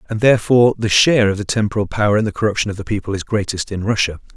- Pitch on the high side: No, low, 105 Hz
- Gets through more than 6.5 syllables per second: Yes, 7.3 syllables/s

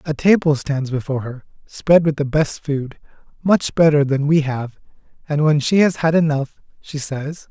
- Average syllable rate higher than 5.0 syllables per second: No, 4.6 syllables/s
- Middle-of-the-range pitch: Yes, medium, 145 Hz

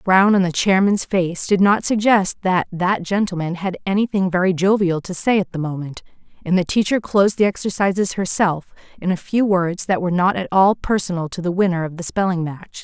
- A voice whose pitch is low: No, medium, 185 Hz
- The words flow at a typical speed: No, fast, 215 wpm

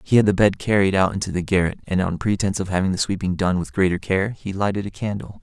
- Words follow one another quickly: Yes, fast, 265 wpm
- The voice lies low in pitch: Yes, very low, 95 Hz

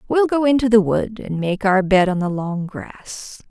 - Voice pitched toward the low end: No, high, 205 Hz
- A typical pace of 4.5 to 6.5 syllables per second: No, 4.3 syllables/s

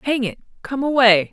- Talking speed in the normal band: Yes, average, 180 wpm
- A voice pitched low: No, high, 245 Hz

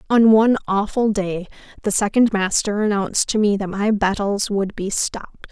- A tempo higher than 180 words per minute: No, average, 175 wpm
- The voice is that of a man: No, female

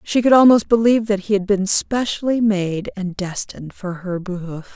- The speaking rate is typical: Yes, average, 190 wpm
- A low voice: No, high, 200 Hz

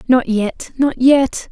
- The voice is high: Yes, very high, 250 Hz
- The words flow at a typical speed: Yes, average, 160 wpm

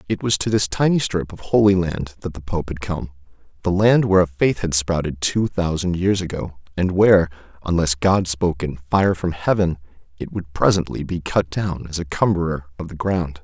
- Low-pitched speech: Yes, very low, 85 Hz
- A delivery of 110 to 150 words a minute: No, average, 200 wpm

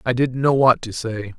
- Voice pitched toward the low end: Yes, low, 125 Hz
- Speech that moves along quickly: Yes, fast, 260 wpm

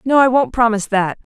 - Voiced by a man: No, female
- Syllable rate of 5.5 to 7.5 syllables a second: Yes, 6.3 syllables/s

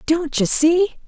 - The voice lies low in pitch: No, very high, 320 Hz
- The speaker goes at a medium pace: Yes, average, 165 wpm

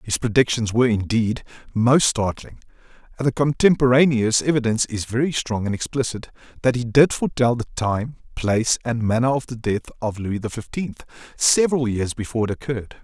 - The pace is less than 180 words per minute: Yes, average, 165 wpm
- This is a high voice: No, low, 120 Hz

